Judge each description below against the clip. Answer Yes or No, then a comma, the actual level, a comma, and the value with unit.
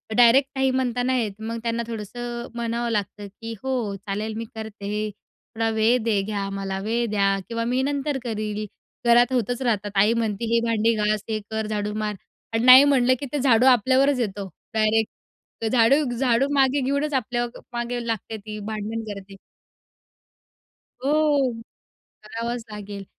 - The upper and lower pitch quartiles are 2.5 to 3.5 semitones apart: Yes, average, 2.8 semitones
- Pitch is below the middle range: No, high, 230 Hz